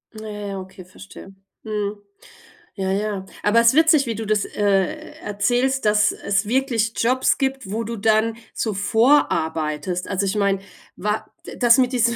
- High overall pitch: Yes, high, 215 Hz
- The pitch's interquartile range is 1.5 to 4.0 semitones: Yes, average, 2.8 semitones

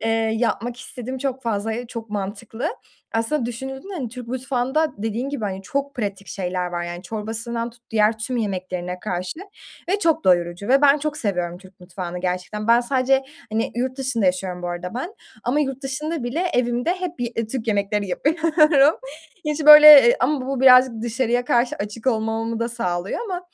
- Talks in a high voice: Yes, high, 235 Hz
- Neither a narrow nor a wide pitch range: Yes, average, 4.8 semitones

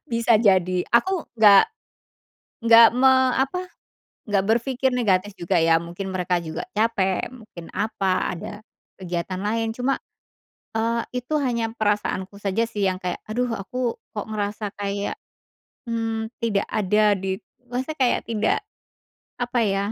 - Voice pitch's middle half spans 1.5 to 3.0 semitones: No, average, 3.4 semitones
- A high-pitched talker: Yes, high, 215 Hz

